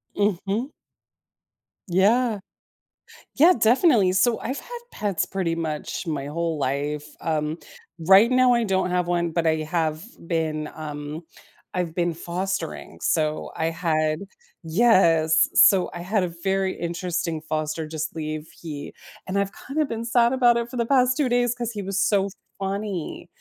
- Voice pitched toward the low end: No, medium, 180 Hz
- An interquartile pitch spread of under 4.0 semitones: No, wide, 5.6 semitones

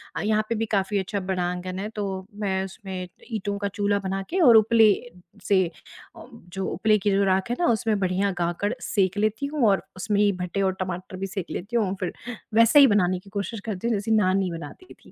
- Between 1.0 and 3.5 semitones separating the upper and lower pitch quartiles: Yes, narrow, 2.4 semitones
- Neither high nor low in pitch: No, high, 200 Hz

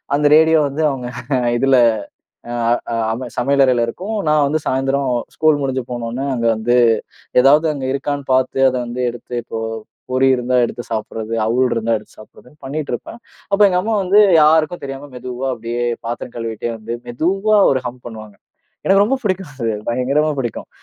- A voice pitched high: No, low, 130 Hz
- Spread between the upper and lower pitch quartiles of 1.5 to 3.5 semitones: No, average, 4.1 semitones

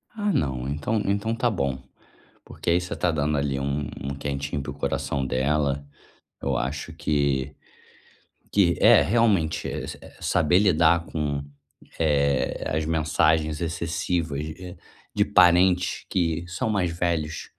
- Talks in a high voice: No, very low, 80 Hz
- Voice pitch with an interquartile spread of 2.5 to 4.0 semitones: Yes, average, 3.7 semitones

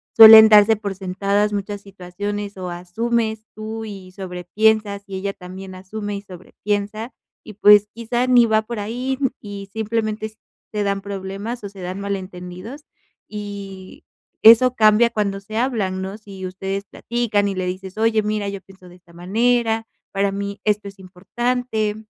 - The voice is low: No, high, 205 Hz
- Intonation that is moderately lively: No, narrow, 2.2 semitones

